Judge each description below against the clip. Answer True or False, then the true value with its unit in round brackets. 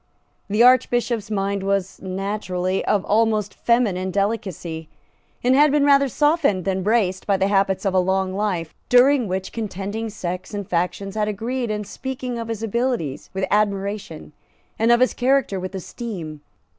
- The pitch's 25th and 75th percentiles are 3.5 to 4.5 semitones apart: True (3.8 semitones)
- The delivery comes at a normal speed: True (155 wpm)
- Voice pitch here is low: False (205 Hz)